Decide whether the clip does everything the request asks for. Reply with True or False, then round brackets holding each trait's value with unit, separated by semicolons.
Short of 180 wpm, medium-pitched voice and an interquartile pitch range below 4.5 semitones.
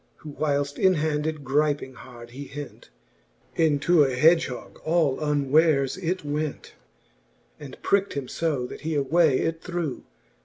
True (145 wpm; 150 Hz; 2.7 semitones)